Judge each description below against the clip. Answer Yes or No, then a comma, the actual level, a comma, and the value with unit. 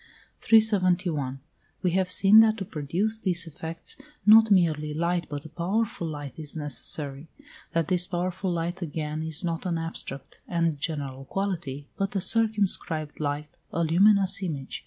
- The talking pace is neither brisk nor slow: Yes, average, 150 wpm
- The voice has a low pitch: No, medium, 170 Hz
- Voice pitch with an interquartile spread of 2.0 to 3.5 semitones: No, average, 4.0 semitones